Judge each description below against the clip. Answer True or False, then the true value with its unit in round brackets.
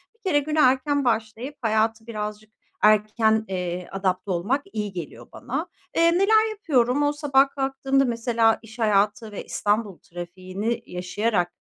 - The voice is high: True (225 Hz)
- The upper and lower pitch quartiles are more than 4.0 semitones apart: True (4.8 semitones)